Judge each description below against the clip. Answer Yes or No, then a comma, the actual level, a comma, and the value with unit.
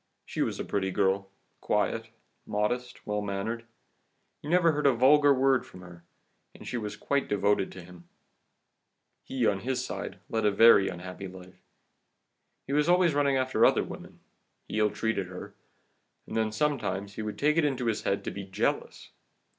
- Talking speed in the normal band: Yes, average, 180 wpm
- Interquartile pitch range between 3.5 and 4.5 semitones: No, wide, 5.4 semitones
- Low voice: Yes, low, 110 Hz